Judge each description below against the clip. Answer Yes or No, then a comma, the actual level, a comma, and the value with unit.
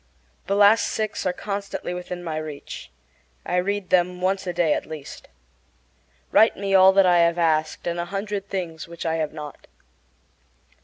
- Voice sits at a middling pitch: Yes, medium, 180 Hz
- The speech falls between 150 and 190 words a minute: Yes, average, 170 wpm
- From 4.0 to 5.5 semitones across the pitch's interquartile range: No, average, 3.0 semitones